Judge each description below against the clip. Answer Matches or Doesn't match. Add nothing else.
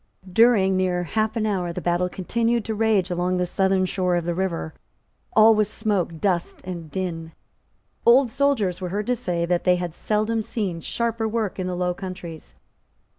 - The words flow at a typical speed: Matches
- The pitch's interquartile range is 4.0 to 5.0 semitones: Doesn't match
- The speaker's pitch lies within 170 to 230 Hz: Matches